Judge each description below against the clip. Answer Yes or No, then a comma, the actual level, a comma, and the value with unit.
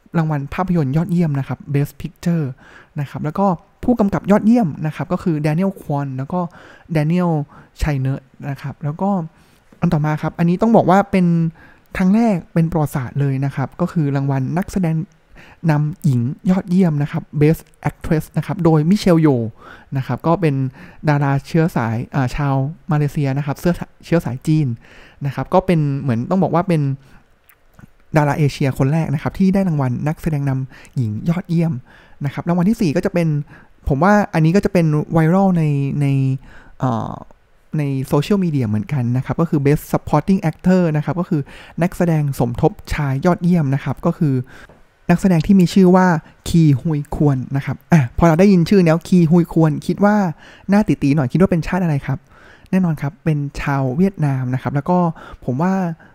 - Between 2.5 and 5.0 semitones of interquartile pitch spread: Yes, average, 4.0 semitones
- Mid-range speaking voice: Yes, medium, 155 Hz